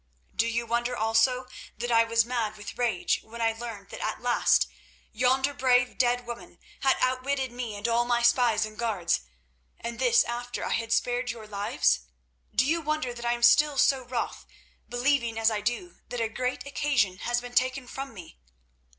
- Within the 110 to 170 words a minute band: No, average, 185 wpm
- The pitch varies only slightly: Yes, narrow, 2.1 semitones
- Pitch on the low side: No, high, 240 Hz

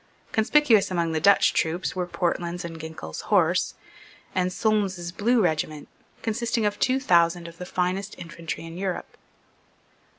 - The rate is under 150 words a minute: Yes, average, 140 wpm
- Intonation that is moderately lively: Yes, average, 3.6 semitones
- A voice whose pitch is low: No, medium, 180 Hz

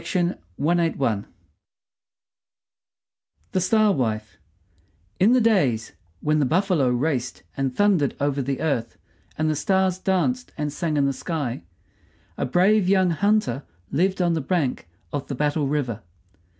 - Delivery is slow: Yes, slow, 125 wpm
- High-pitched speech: No, medium, 155 Hz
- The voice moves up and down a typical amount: No, wide, 5.7 semitones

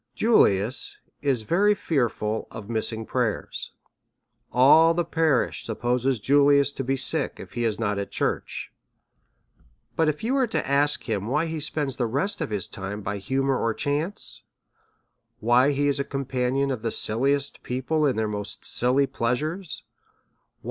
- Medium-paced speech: Yes, average, 160 wpm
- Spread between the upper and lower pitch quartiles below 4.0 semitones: No, average, 4.4 semitones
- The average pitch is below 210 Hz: Yes, low, 135 Hz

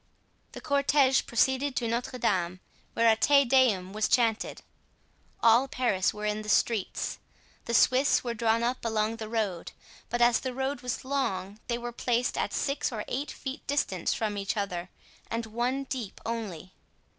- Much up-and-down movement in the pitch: No, average, 3.4 semitones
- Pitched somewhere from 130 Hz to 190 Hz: No, high, 235 Hz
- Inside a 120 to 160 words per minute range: No, average, 170 wpm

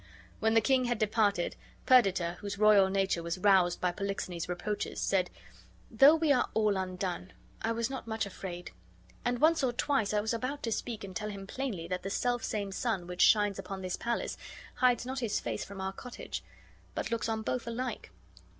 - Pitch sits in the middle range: No, high, 210 Hz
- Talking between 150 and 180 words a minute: No, average, 190 wpm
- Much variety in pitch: No, average, 3.9 semitones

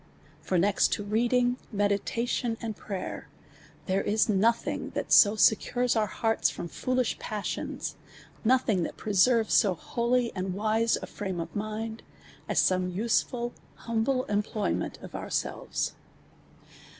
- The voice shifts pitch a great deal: No, average, 2.7 semitones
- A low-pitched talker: No, high, 220 Hz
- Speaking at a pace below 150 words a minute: Yes, slow, 135 wpm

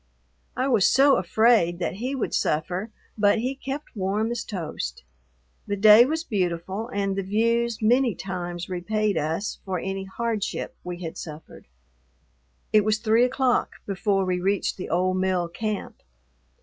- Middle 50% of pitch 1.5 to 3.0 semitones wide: No, average, 4.1 semitones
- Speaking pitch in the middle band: No, high, 200 Hz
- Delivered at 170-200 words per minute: No, average, 150 wpm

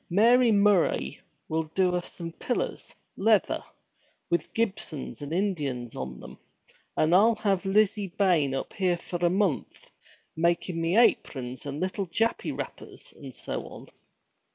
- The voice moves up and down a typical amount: Yes, average, 4.5 semitones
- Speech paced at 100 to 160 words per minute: Yes, average, 140 wpm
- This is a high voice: No, medium, 180 Hz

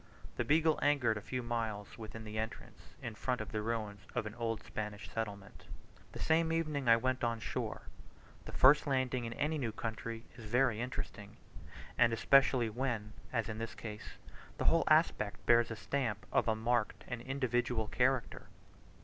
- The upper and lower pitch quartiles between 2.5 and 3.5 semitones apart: Yes, average, 3.0 semitones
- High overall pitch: No, low, 115 Hz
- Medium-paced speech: Yes, average, 175 wpm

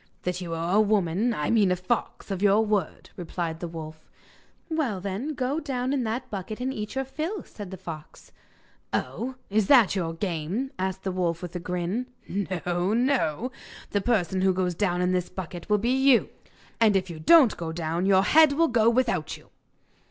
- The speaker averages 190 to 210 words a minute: Yes, average, 195 wpm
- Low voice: No, high, 195 Hz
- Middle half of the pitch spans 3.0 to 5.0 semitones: No, wide, 5.5 semitones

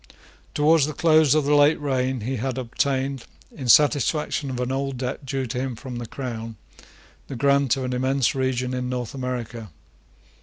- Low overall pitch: Yes, low, 130 Hz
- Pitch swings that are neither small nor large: No, narrow, 1.9 semitones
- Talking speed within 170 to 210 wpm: Yes, average, 180 wpm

